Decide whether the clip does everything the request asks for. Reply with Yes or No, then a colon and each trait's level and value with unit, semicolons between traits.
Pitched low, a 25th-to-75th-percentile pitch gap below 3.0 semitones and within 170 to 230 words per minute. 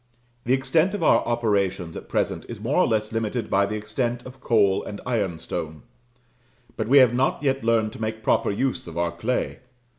No: low, 115 Hz; average, 3.9 semitones; average, 190 wpm